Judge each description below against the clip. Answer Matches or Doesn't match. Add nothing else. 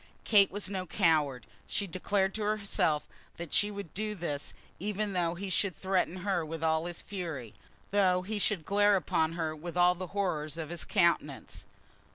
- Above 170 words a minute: Matches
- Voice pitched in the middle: Matches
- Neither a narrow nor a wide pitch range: Matches